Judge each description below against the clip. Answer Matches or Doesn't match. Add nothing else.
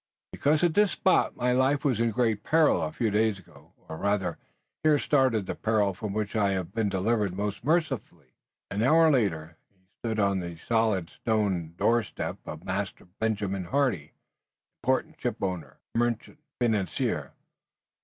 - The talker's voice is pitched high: Doesn't match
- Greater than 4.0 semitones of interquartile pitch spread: Matches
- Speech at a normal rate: Matches